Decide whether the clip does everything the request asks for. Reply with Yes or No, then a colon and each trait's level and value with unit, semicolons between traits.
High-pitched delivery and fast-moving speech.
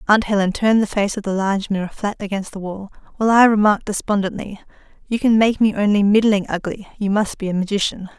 Yes: high, 205 Hz; fast, 215 wpm